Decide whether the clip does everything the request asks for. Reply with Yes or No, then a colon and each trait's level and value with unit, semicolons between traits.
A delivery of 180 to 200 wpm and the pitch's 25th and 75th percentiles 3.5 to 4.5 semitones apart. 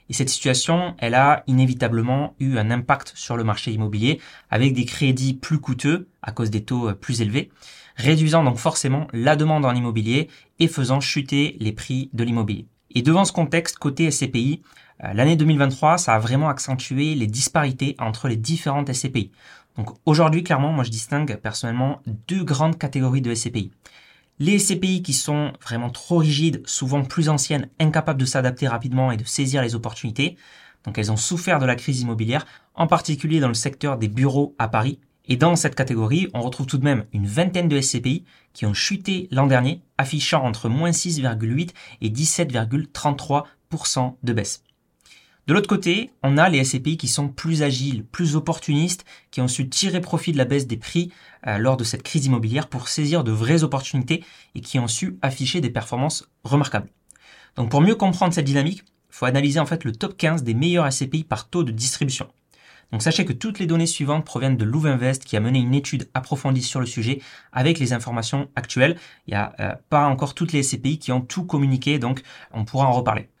Yes: average, 190 wpm; average, 4.0 semitones